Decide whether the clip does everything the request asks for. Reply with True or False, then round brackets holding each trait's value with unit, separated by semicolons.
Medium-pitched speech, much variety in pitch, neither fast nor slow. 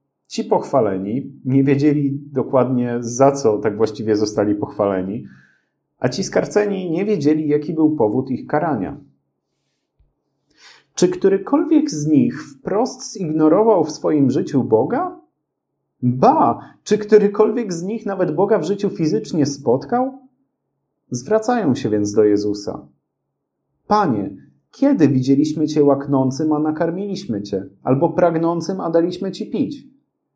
True (155 Hz; 7.0 semitones; 120 wpm)